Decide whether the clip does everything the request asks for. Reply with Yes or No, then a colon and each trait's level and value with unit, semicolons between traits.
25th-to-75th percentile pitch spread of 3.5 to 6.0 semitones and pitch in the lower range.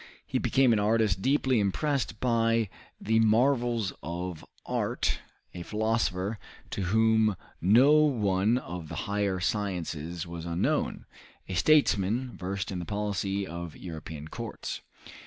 Yes: average, 4.2 semitones; low, 105 Hz